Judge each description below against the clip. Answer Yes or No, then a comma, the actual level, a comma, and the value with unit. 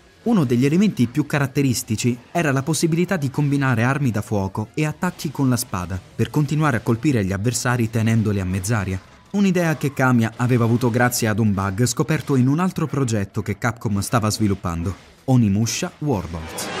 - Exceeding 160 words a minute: Yes, fast, 170 wpm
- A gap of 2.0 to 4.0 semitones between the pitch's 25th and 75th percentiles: No, wide, 5.6 semitones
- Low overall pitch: Yes, low, 125 Hz